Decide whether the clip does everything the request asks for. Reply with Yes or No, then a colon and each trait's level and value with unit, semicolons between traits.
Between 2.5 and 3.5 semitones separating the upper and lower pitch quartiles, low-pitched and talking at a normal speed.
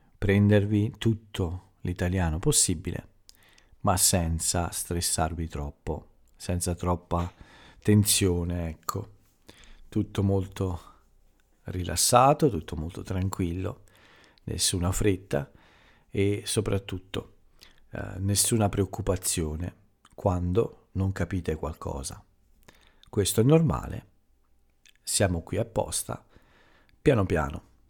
No: average, 2.8 semitones; very low, 95 Hz; slow, 80 wpm